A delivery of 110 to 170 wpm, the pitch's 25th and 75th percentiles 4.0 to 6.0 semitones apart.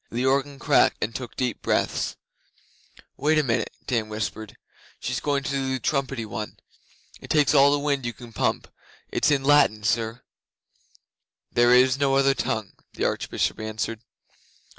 No: average, 160 wpm; average, 3.4 semitones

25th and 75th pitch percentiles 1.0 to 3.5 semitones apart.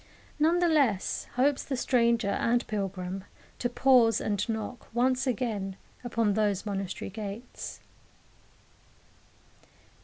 No: average, 3.9 semitones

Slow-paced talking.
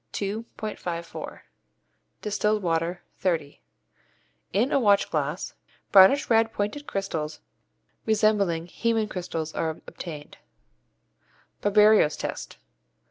Yes: slow, 85 wpm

